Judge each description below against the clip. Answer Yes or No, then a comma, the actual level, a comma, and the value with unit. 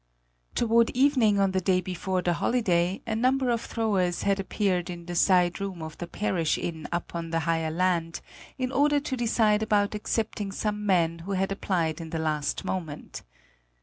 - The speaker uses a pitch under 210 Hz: Yes, high, 190 Hz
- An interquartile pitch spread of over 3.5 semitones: Yes, average, 4.2 semitones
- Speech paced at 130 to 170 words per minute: No, average, 180 wpm